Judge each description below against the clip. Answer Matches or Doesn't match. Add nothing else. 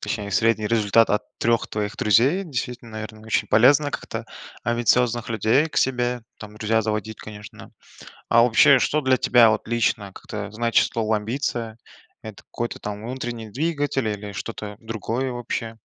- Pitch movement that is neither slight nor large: Doesn't match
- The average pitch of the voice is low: Matches